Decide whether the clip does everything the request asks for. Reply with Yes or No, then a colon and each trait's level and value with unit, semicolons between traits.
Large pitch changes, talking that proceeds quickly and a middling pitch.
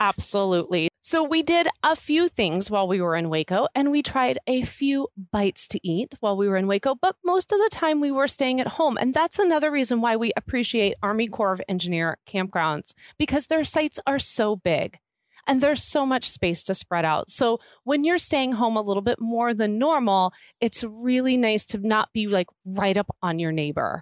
No: wide, 6.6 semitones; fast, 210 wpm; high, 230 Hz